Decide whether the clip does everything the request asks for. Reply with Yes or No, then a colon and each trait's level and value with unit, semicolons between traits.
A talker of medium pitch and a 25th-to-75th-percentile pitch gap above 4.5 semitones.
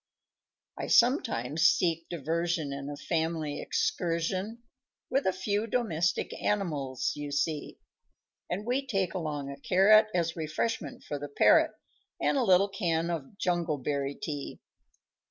Yes: medium, 170 Hz; average, 5.1 semitones